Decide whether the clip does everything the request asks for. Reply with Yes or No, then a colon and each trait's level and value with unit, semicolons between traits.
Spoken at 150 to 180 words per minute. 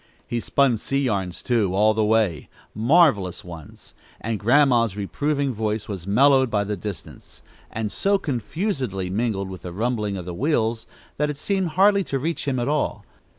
Yes: average, 170 wpm